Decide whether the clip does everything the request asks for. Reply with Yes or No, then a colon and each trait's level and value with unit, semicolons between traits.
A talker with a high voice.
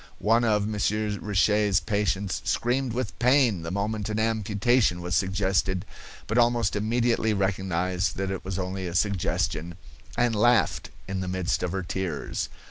No: low, 100 Hz